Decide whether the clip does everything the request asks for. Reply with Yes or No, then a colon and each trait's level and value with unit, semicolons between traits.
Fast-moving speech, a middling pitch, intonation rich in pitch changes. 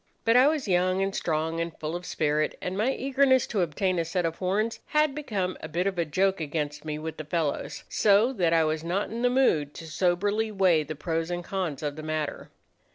No: fast, 225 wpm; medium, 175 Hz; average, 4.6 semitones